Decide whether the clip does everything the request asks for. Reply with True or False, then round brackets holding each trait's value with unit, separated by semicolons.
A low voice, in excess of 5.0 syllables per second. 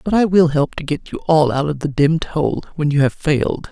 False (155 Hz; 5.4 syllables/s)